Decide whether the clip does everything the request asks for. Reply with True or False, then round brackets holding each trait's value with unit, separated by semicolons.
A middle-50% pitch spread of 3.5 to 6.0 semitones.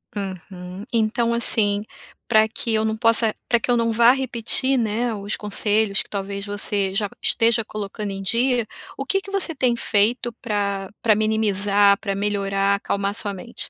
False (2.7 semitones)